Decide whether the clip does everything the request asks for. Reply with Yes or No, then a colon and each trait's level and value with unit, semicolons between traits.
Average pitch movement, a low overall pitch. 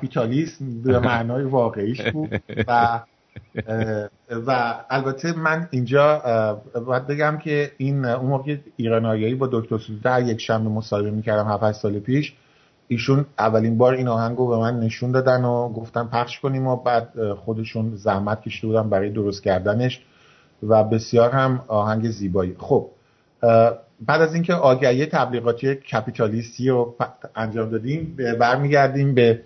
Yes: average, 3.1 semitones; low, 120 Hz